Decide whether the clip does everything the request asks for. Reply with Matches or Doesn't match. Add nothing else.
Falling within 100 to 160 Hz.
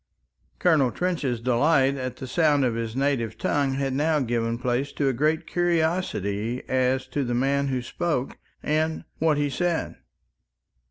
Matches